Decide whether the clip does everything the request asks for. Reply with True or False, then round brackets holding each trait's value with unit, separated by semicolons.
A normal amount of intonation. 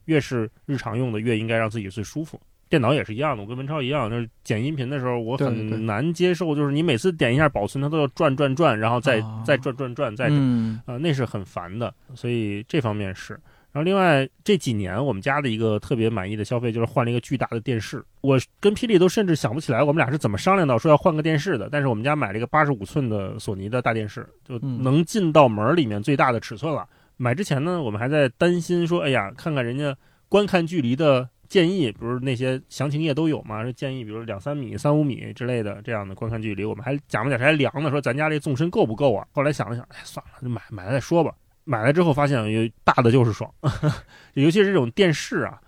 True (4.8 semitones)